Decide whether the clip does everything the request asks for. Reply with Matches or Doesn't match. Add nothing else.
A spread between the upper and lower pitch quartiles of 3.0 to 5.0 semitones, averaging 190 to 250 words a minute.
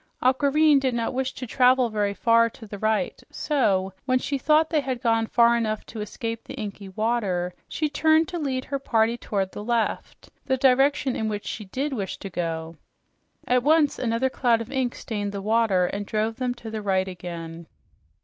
Matches